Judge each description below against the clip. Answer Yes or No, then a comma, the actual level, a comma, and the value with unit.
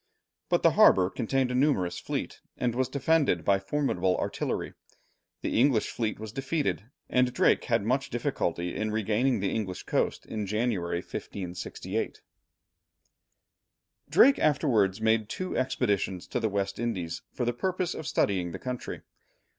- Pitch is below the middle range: Yes, low, 110 Hz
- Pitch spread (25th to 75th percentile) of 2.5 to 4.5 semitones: No, average, 5.1 semitones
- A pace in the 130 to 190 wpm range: Yes, average, 145 wpm